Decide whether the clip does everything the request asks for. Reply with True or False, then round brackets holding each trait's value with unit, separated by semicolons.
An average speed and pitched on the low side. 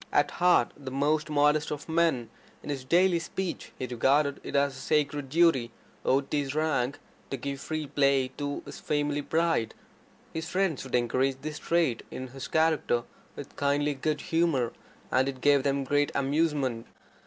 False (170 wpm; 145 Hz)